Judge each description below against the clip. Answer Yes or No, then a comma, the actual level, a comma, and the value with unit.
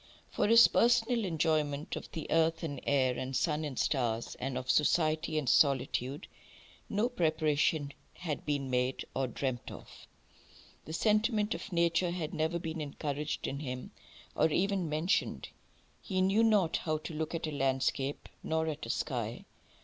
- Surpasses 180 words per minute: No, average, 160 wpm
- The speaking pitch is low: No, medium, 155 Hz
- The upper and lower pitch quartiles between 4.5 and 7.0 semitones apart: No, average, 3.6 semitones